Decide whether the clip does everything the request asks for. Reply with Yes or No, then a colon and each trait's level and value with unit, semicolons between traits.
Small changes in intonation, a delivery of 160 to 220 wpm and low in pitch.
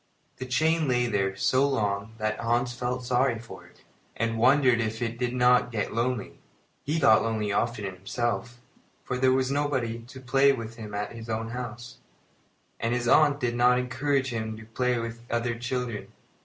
Yes: narrow, 2.1 semitones; average, 180 wpm; low, 120 Hz